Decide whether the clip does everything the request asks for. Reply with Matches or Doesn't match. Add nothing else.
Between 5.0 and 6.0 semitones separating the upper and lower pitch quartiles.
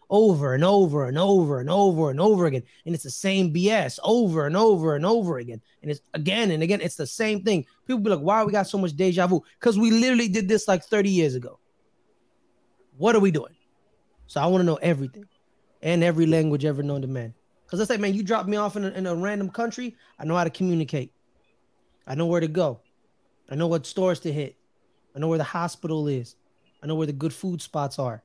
Matches